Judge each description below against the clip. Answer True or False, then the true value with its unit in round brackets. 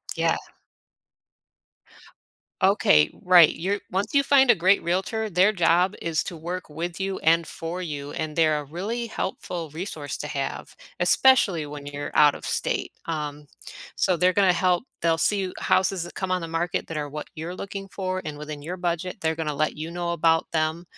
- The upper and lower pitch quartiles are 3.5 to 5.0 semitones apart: False (3.1 semitones)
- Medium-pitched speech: True (170 Hz)